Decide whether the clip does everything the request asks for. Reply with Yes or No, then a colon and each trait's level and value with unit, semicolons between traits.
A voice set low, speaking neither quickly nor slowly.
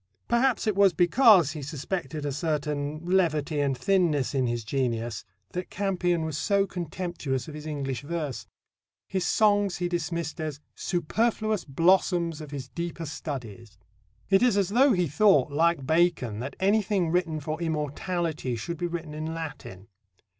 No: medium, 165 Hz; average, 155 wpm